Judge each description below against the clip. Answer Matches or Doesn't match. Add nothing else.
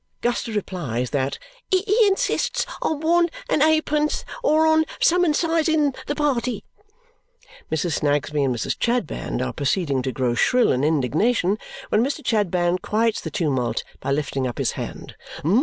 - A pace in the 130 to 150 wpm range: Matches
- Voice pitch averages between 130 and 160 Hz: Doesn't match